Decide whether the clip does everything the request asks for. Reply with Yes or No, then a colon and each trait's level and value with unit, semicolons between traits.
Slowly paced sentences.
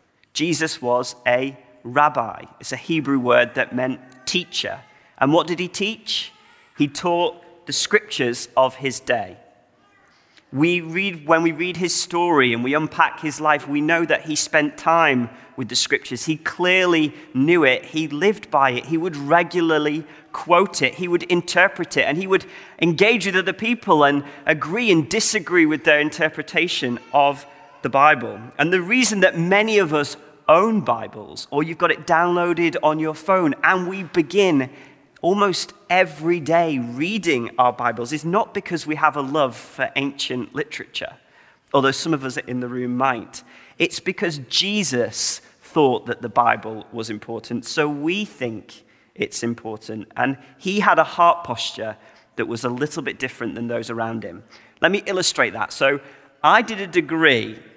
No: average, 165 wpm